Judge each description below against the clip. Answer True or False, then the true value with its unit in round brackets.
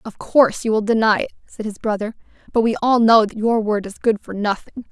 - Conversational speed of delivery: False (245 wpm)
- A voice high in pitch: True (220 Hz)